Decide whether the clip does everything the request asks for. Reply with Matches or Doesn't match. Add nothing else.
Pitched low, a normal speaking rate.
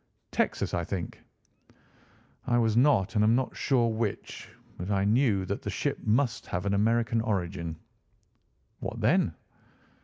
Matches